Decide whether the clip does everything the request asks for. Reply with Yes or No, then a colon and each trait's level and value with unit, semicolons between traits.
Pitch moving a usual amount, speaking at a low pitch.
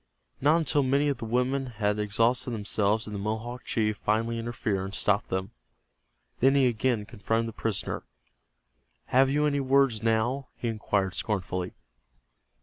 Yes: average, 3.7 semitones; low, 115 Hz